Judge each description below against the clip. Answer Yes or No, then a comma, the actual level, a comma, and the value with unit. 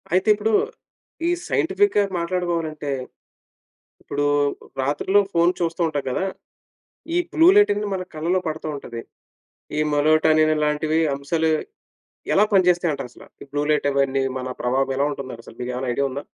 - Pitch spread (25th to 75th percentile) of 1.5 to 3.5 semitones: No, average, 4.3 semitones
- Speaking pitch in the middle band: Yes, medium, 155 Hz